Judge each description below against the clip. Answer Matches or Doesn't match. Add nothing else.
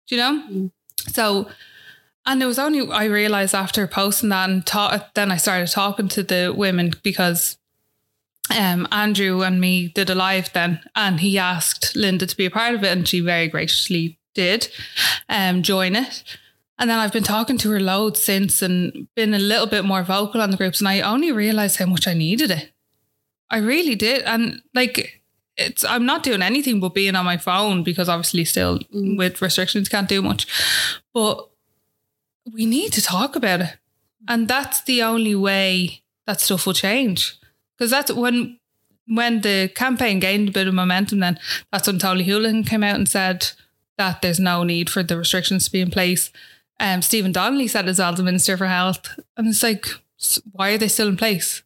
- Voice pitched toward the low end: Doesn't match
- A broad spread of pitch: Doesn't match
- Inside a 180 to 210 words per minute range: Matches